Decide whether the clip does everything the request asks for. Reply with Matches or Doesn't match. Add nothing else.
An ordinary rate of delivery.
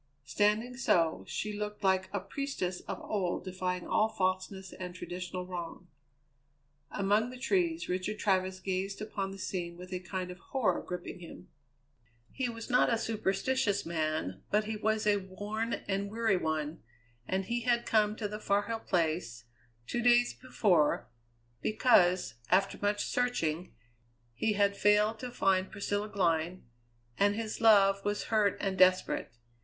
Matches